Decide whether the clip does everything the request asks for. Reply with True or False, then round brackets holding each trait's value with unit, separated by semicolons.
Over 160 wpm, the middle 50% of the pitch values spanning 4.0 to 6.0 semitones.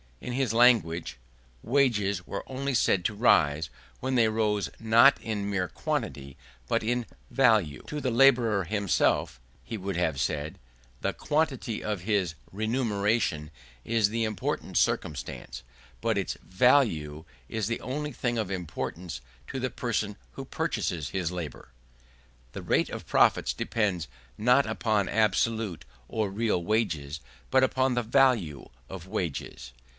False (140 wpm; 5.2 semitones)